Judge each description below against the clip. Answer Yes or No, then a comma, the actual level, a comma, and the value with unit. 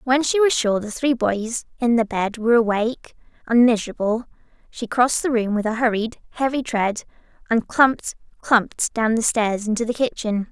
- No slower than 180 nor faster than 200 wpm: Yes, average, 185 wpm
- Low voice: No, high, 230 Hz